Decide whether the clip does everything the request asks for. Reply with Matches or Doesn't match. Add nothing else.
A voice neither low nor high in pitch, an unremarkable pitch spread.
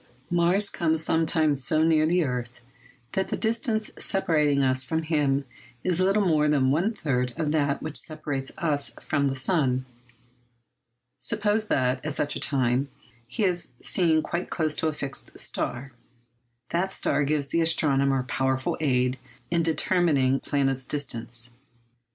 Matches